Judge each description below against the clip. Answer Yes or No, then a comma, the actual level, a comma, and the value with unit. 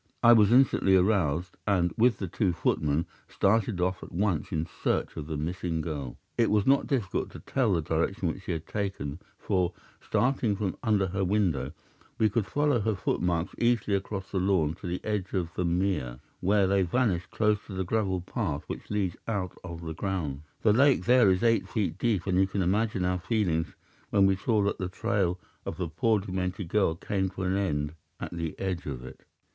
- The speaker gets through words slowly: No, average, 200 wpm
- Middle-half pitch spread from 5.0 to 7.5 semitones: No, average, 3.5 semitones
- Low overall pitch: Yes, very low, 95 Hz